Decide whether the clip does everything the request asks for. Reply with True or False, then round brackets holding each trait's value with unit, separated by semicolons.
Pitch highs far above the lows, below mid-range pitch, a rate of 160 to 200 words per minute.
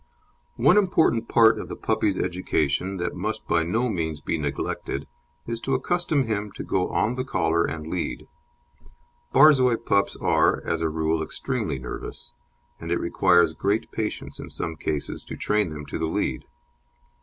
True (6.3 semitones; 95 Hz; 165 wpm)